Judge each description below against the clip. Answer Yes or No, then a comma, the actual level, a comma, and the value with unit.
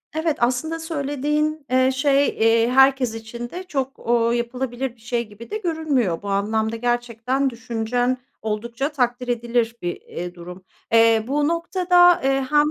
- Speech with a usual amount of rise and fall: Yes, average, 3.9 semitones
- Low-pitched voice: No, high, 245 Hz